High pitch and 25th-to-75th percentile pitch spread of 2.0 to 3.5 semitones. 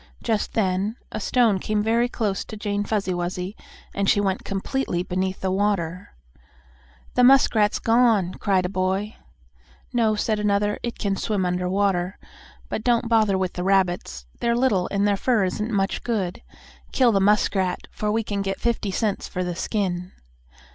Yes: high, 200 Hz; average, 2.7 semitones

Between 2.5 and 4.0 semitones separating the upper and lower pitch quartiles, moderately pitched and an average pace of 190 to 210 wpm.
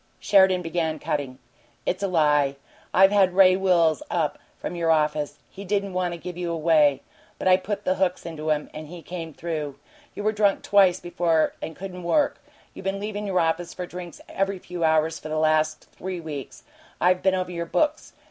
Yes: average, 3.3 semitones; medium, 175 Hz; average, 195 wpm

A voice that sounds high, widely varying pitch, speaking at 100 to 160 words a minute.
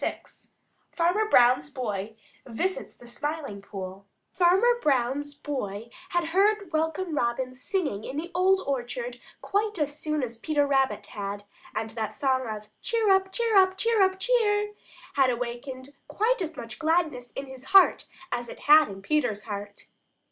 Yes: very high, 290 Hz; wide, 7.8 semitones; average, 155 wpm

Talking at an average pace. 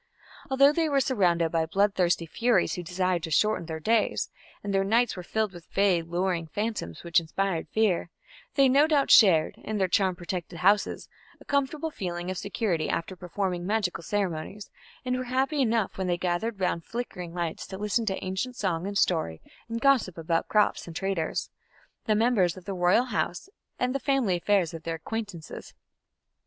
Yes: average, 180 wpm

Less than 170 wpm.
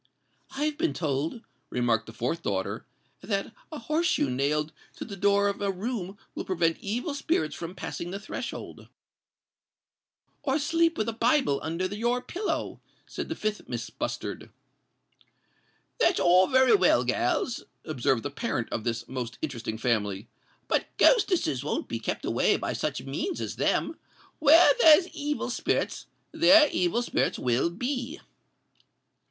Yes: average, 145 wpm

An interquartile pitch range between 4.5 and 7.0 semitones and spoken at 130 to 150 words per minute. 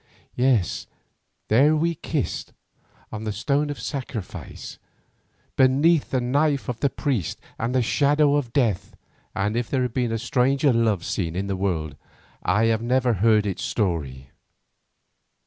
Yes: average, 5.0 semitones; average, 145 wpm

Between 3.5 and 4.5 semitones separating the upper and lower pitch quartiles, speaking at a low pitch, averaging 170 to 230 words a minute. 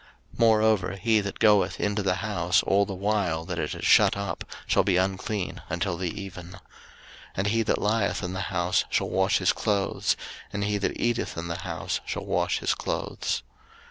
No: narrow, 2.4 semitones; low, 100 Hz; average, 195 wpm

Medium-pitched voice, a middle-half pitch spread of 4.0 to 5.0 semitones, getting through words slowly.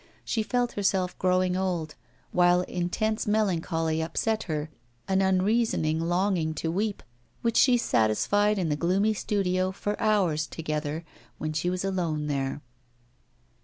Yes: medium, 180 Hz; average, 4.3 semitones; slow, 130 wpm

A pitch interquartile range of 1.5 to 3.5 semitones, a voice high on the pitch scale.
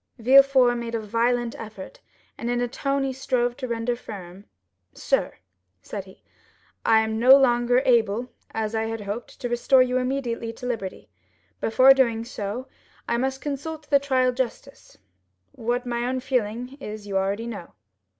Yes: narrow, 2.6 semitones; high, 240 Hz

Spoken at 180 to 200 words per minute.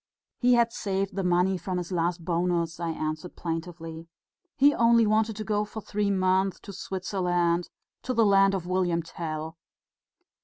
No: average, 160 wpm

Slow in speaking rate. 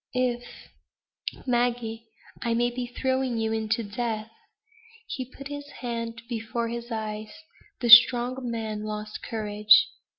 Yes: slow, 130 wpm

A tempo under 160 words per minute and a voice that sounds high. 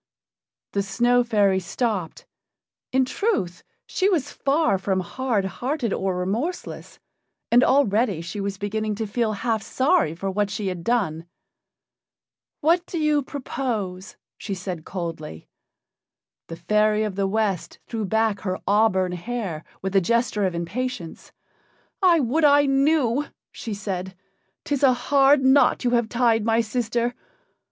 Yes: average, 140 wpm; high, 220 Hz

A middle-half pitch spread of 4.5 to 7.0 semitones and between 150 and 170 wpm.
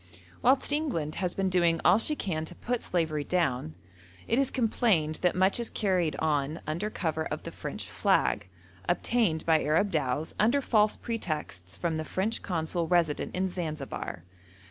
Yes: average, 5.1 semitones; average, 165 wpm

